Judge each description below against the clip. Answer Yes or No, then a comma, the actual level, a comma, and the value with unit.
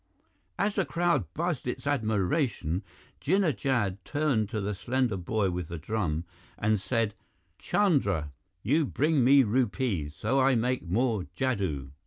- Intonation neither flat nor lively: No, wide, 6.0 semitones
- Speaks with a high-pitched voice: No, low, 115 Hz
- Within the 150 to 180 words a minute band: No, average, 140 wpm